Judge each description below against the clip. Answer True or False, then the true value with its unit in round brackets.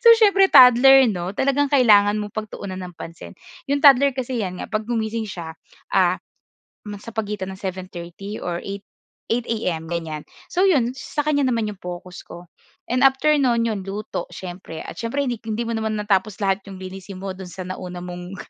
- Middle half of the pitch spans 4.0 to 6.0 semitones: True (4.8 semitones)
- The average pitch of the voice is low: False (210 Hz)